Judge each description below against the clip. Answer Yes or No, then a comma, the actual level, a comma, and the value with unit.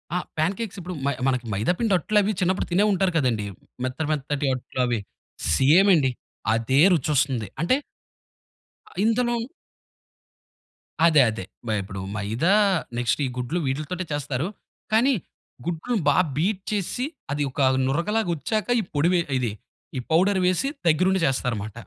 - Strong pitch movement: Yes, wide, 6.8 semitones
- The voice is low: No, medium, 155 Hz